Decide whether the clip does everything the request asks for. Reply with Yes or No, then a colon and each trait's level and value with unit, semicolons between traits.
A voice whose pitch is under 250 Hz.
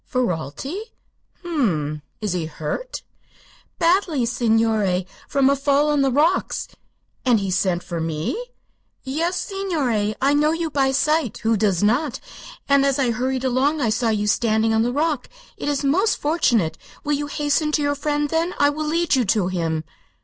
No: very high, 265 Hz